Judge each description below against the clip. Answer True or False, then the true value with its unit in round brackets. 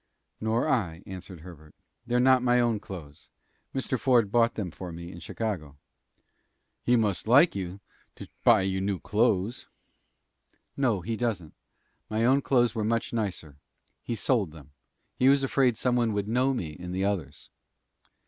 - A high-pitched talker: False (110 Hz)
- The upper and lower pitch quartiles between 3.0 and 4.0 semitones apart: False (5.1 semitones)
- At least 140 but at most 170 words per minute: True (160 wpm)